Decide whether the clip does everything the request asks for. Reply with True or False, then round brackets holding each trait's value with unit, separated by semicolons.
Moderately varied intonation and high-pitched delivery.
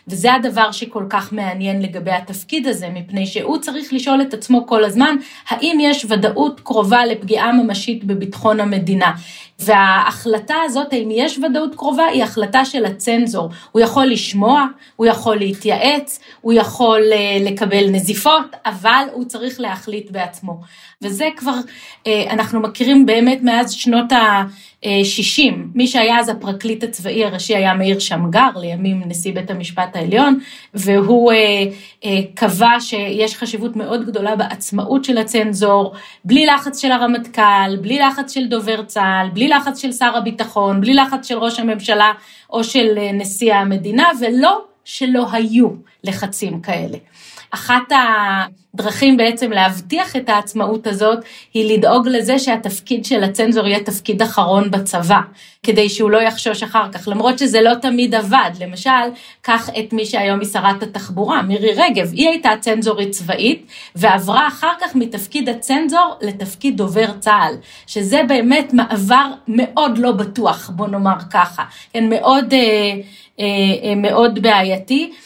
True (3.7 semitones; 220 Hz)